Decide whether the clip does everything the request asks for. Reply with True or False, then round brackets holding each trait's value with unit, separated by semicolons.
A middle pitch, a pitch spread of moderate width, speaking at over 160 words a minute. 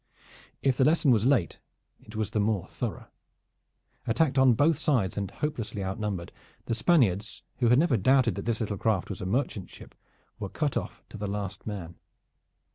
False (110 Hz; 4.9 semitones; 180 wpm)